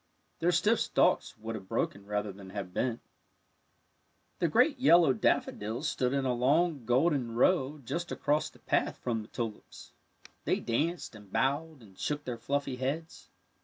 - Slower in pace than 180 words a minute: Yes, average, 160 wpm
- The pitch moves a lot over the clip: Yes, wide, 6.0 semitones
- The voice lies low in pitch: Yes, low, 130 Hz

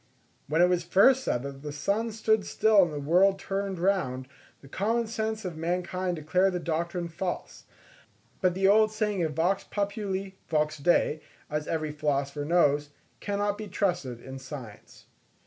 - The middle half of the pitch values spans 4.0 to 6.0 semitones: Yes, average, 4.8 semitones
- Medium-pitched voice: Yes, medium, 180 Hz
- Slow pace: No, average, 165 wpm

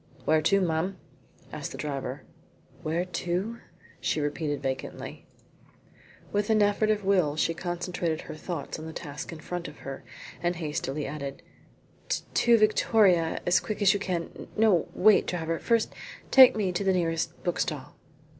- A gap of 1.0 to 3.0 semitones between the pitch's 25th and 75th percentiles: No, average, 4.2 semitones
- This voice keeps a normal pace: Yes, average, 155 wpm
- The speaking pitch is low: No, medium, 175 Hz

